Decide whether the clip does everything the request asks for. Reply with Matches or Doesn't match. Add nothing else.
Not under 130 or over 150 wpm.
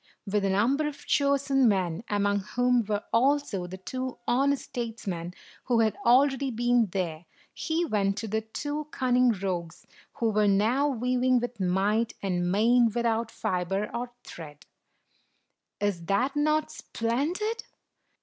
Matches